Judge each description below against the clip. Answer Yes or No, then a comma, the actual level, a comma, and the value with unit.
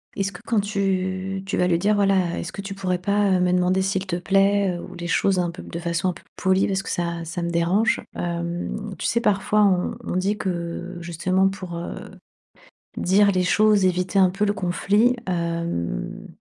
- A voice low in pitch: No, medium, 185 Hz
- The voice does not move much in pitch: Yes, narrow, 2.3 semitones